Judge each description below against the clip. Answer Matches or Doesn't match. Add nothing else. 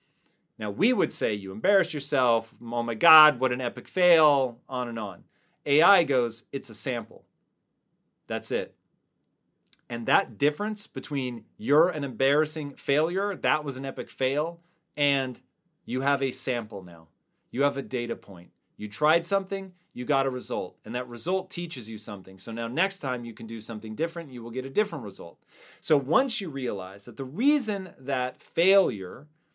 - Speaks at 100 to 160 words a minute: Doesn't match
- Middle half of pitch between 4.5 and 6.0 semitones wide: Matches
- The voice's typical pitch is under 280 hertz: Matches